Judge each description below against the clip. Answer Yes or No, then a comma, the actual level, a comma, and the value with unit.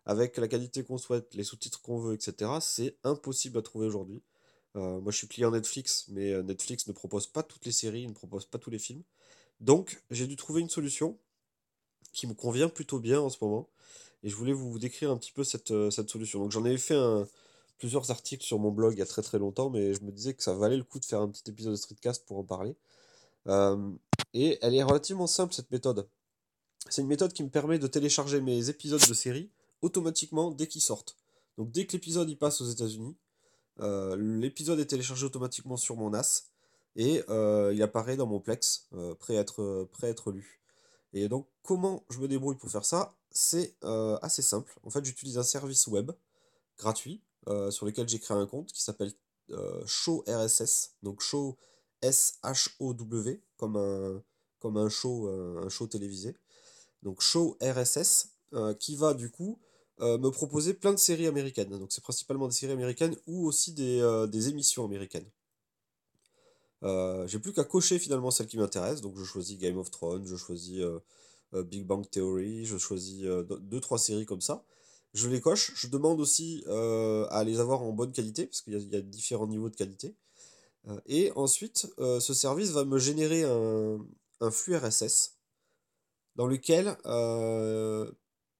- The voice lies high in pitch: No, low, 120 Hz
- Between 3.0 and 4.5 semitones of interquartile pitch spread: No, average, 5.1 semitones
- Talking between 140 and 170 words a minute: No, average, 195 wpm